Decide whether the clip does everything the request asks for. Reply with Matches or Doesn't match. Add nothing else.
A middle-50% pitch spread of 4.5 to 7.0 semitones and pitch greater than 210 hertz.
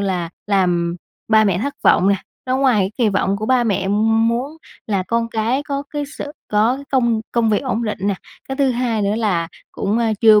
Doesn't match